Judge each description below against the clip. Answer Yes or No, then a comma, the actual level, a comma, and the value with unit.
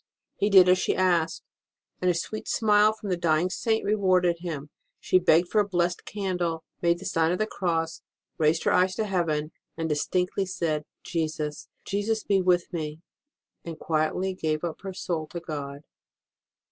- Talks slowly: No, average, 170 wpm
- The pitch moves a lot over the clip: No, average, 2.9 semitones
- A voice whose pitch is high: No, medium, 175 Hz